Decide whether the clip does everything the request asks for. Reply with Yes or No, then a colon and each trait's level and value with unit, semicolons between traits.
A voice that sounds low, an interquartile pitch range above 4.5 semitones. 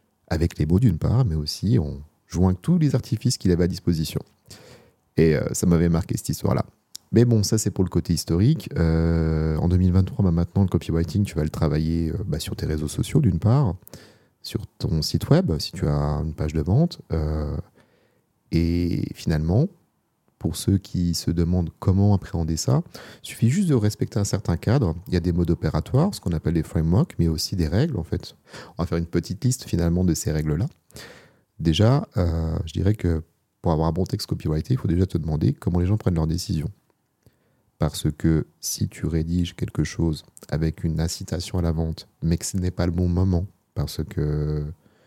No: very low, 85 Hz; average, 4.1 semitones